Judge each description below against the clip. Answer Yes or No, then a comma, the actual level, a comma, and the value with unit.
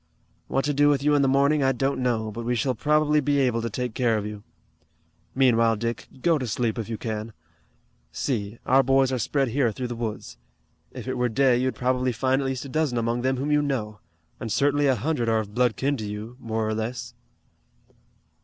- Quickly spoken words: Yes, fast, 220 wpm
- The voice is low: Yes, low, 125 Hz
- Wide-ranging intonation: No, average, 3.2 semitones